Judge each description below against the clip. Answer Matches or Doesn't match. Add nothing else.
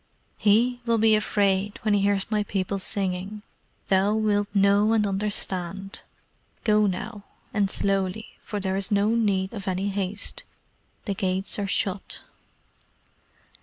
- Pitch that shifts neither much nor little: Doesn't match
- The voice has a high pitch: Matches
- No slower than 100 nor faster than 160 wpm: Matches